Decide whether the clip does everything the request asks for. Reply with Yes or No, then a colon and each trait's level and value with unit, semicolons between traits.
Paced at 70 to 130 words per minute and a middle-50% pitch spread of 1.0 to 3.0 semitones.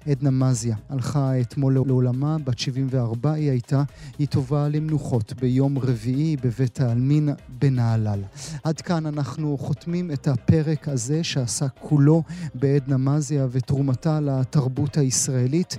Yes: average, 120 wpm; narrow, 2.5 semitones